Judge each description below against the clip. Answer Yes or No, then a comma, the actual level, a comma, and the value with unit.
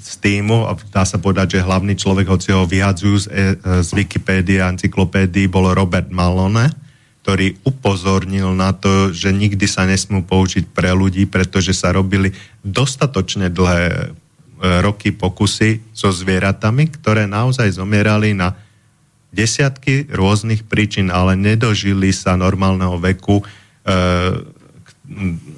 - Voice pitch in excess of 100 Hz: No, very low, 95 Hz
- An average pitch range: No, narrow, 2.0 semitones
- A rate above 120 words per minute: Yes, average, 130 wpm